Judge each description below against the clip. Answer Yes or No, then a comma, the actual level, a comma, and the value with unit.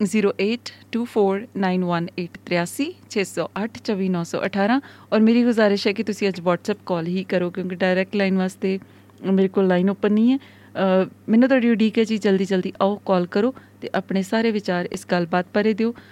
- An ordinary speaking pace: Yes, average, 145 wpm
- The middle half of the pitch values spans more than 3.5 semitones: No, average, 2.8 semitones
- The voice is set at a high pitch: Yes, high, 195 Hz